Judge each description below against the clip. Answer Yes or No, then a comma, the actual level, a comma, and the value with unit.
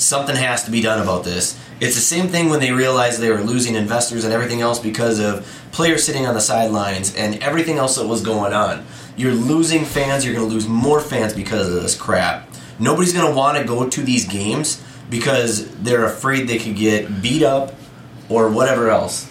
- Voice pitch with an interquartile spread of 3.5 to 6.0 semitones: Yes, average, 4.0 semitones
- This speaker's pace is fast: Yes, fast, 210 wpm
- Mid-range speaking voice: No, low, 120 Hz